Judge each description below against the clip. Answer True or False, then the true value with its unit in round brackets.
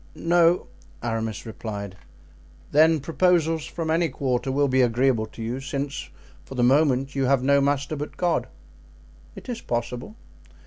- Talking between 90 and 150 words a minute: True (145 wpm)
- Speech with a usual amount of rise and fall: True (4.4 semitones)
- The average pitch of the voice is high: False (135 Hz)